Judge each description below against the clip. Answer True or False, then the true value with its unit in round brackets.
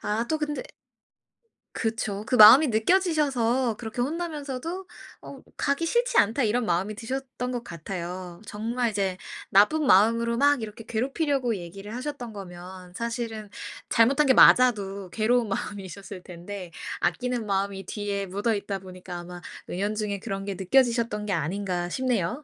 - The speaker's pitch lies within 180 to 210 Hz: False (220 Hz)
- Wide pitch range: False (4.5 semitones)